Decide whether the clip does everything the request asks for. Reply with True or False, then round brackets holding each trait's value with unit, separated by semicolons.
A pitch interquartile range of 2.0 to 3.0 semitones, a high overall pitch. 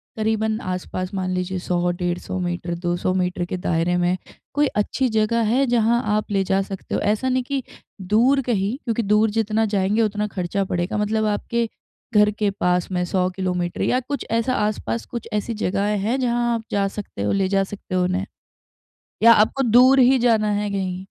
False (3.7 semitones; 205 Hz)